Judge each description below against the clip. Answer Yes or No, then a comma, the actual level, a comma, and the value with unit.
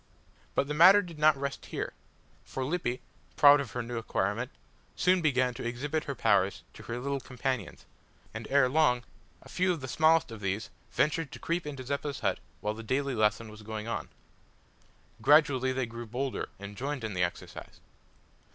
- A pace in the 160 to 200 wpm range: Yes, average, 180 wpm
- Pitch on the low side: Yes, low, 130 Hz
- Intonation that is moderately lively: Yes, average, 4.4 semitones